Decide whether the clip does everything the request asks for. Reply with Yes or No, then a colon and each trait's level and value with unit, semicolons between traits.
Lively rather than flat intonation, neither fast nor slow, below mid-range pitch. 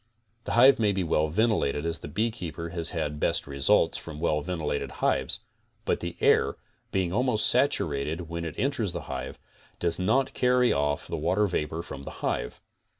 Yes: wide, 6.0 semitones; average, 175 wpm; very low, 85 Hz